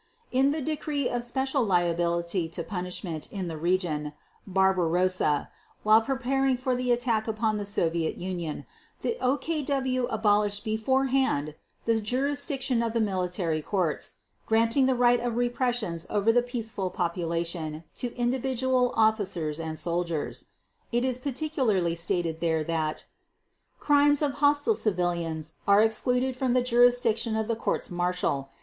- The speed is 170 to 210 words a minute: No, slow, 135 wpm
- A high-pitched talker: Yes, high, 220 Hz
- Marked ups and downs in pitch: Yes, wide, 6.5 semitones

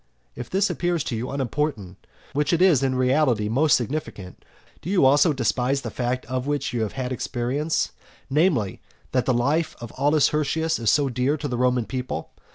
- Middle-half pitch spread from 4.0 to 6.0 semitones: No, average, 3.5 semitones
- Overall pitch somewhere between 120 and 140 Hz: Yes, low, 135 Hz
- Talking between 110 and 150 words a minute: No, average, 180 wpm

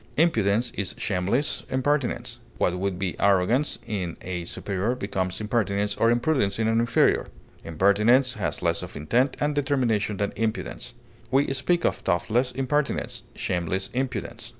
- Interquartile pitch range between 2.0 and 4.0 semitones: No, average, 5.2 semitones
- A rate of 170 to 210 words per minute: No, average, 140 wpm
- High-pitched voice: No, low, 110 Hz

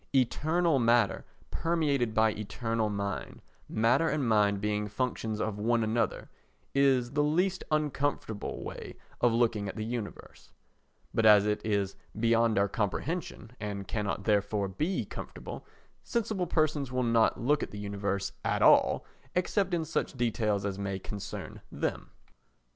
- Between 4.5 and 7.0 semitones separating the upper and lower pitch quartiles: Yes, average, 5.2 semitones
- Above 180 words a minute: No, average, 140 wpm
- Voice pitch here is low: Yes, low, 115 Hz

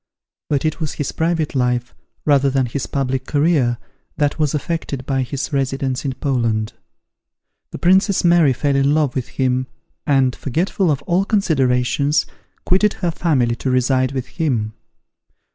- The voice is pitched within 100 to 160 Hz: Yes, medium, 140 Hz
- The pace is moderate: Yes, average, 150 wpm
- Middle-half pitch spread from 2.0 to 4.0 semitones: Yes, average, 3.5 semitones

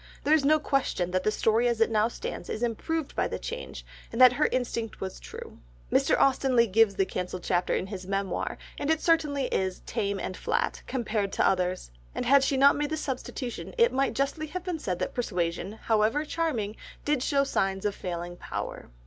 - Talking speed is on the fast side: Yes, fast, 210 wpm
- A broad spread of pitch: Yes, wide, 6.5 semitones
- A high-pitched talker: Yes, high, 235 Hz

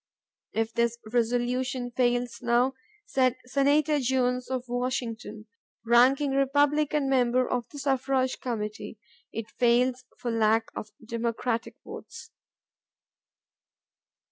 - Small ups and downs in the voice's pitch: Yes, narrow, 2.1 semitones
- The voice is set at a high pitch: Yes, very high, 250 Hz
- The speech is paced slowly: Yes, slow, 100 wpm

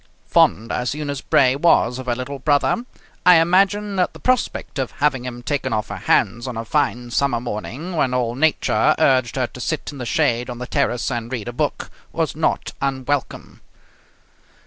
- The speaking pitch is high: No, low, 130 Hz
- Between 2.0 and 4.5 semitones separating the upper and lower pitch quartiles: Yes, average, 3.3 semitones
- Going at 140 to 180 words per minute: No, average, 190 wpm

